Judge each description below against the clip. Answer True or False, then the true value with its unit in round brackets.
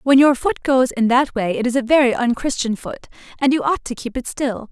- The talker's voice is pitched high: True (255 Hz)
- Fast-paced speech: True (255 wpm)